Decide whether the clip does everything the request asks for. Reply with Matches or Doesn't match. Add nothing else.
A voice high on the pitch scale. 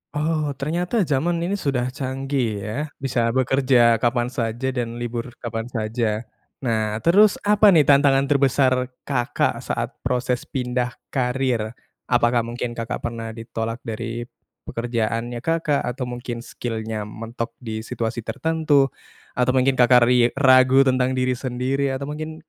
Doesn't match